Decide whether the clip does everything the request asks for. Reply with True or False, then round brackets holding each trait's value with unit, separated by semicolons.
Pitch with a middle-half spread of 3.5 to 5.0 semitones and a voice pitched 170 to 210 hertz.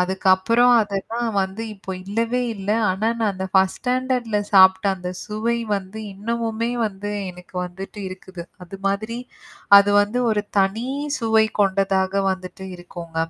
False (3.0 semitones; 200 Hz)